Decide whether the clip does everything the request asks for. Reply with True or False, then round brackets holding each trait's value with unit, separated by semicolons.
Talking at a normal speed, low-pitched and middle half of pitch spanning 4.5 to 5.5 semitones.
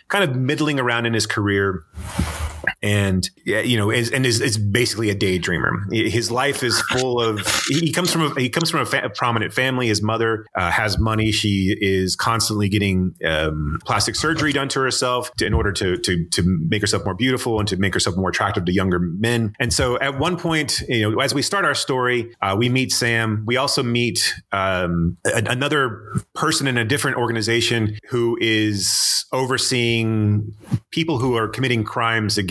False (195 wpm; 115 Hz; 3.9 semitones)